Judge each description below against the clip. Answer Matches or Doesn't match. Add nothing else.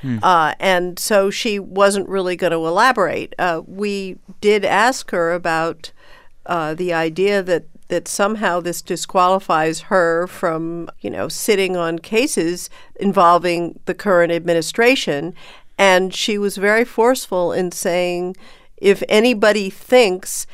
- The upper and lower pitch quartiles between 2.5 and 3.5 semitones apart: Matches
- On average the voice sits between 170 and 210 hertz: Matches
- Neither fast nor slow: Doesn't match